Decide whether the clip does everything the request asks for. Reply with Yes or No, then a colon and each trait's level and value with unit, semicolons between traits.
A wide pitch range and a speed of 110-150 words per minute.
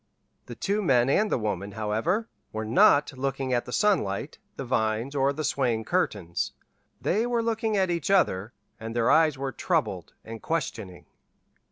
No: wide, 8.0 semitones; average, 165 wpm